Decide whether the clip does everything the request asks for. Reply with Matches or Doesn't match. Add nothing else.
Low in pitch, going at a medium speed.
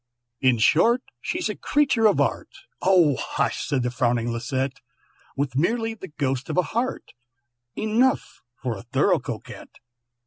Doesn't match